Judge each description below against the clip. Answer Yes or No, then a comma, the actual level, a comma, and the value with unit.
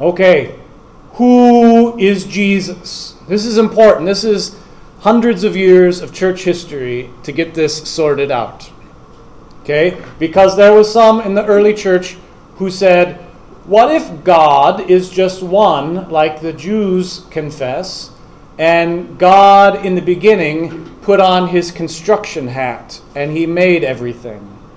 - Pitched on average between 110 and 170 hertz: No, medium, 185 Hz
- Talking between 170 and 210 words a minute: No, slow, 135 wpm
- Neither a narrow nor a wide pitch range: Yes, average, 3.8 semitones